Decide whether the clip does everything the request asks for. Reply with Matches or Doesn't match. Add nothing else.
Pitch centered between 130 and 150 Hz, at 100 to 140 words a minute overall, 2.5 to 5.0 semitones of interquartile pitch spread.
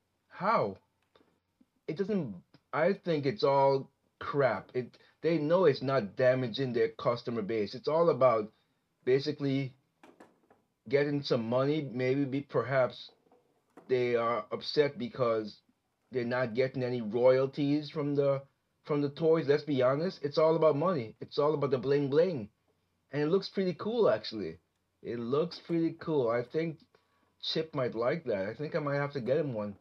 Doesn't match